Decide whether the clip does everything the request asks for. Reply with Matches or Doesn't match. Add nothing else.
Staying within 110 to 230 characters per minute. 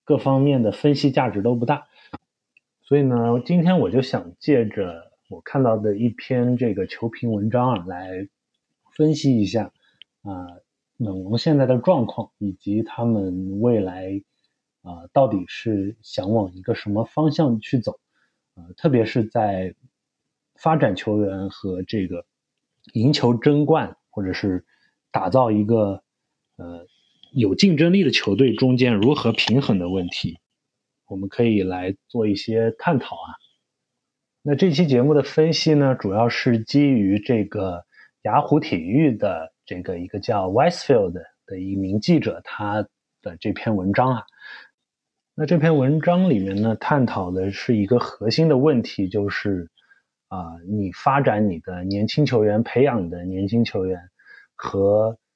Matches